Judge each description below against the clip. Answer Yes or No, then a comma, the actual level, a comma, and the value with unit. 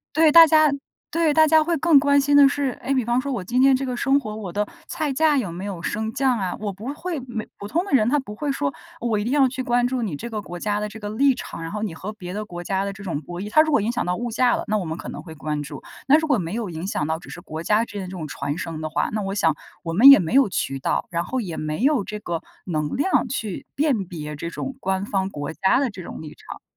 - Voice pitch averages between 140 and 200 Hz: No, high, 215 Hz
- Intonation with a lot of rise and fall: Yes, wide, 7.4 semitones